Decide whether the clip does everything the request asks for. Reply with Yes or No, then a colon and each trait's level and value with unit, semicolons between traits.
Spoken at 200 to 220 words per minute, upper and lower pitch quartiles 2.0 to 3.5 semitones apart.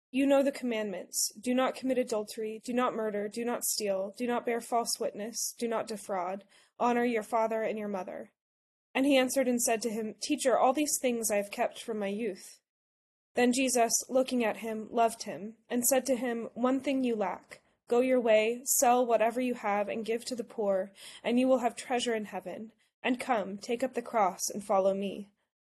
Yes: fast, 205 wpm; average, 3.0 semitones